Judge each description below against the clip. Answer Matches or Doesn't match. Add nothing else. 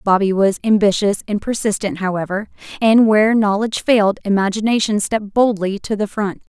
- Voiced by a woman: Matches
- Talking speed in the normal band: Matches